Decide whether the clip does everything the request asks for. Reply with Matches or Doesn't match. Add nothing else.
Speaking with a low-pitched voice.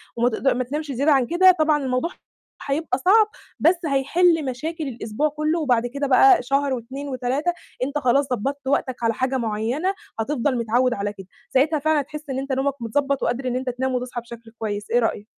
Doesn't match